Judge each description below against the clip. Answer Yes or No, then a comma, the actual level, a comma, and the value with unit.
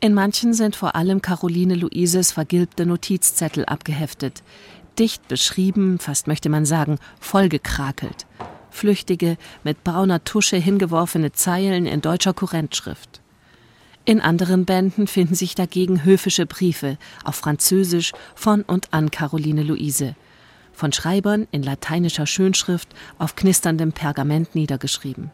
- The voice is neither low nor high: Yes, medium, 175 Hz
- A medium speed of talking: No, slow, 120 wpm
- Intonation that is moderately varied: Yes, average, 3.7 semitones